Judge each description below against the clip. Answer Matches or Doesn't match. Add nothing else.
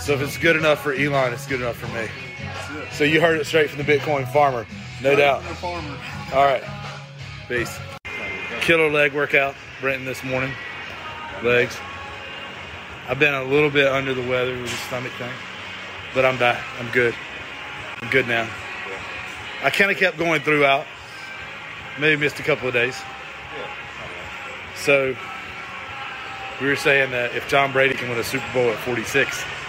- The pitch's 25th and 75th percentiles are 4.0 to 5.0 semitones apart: Doesn't match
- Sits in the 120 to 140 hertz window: Matches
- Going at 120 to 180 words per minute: Matches